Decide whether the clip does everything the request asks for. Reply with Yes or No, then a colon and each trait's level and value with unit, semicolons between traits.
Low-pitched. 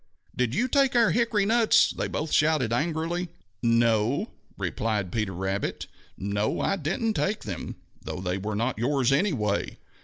Yes: low, 130 Hz